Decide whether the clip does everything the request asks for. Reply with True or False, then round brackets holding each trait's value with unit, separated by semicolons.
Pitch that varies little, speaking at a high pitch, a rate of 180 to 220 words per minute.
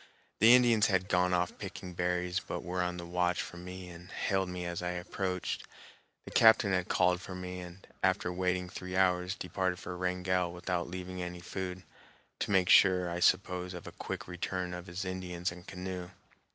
False (0.7 semitones; 90 Hz; 190 wpm)